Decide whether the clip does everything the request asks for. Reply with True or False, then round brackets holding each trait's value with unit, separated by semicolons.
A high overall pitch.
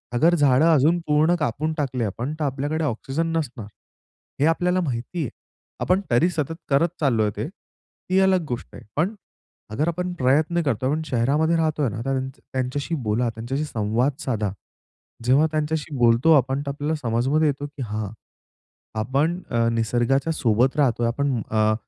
False (140 Hz)